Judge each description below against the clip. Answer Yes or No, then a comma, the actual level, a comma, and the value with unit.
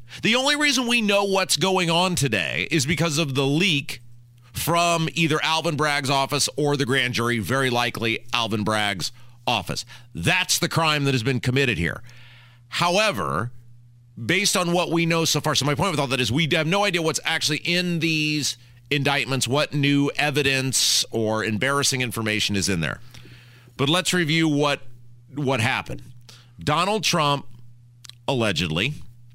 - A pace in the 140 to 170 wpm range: Yes, average, 160 wpm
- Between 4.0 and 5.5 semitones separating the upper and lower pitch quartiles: Yes, average, 5.2 semitones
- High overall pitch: No, medium, 140 Hz